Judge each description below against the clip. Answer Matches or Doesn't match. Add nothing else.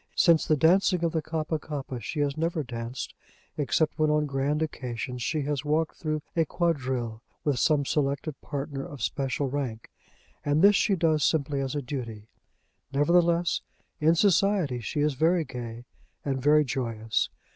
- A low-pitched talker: Doesn't match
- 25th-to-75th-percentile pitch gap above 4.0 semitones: Doesn't match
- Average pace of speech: Matches